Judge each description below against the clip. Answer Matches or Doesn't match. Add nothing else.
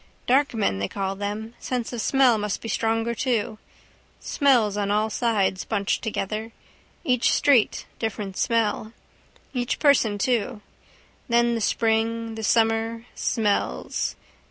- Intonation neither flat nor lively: Doesn't match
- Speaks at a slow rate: Matches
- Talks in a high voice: Matches